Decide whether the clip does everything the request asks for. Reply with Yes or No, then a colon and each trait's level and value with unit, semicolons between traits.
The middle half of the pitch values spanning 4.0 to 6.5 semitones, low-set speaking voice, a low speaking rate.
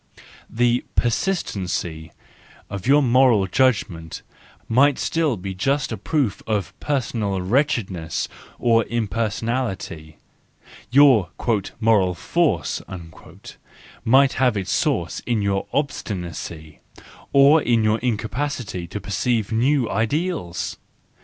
Yes: wide, 5.5 semitones; low, 115 Hz; slow, 95 wpm